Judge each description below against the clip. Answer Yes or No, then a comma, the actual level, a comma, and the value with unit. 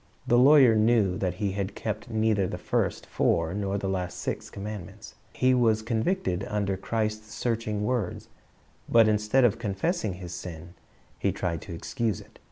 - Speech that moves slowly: No, average, 165 wpm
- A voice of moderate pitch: No, low, 105 Hz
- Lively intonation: No, average, 3.3 semitones